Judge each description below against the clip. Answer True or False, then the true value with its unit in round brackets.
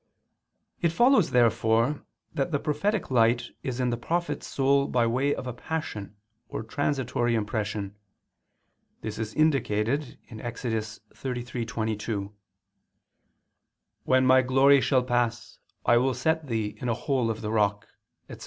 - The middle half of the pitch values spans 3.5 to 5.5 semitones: True (3.8 semitones)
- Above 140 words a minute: False (135 wpm)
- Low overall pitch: True (120 Hz)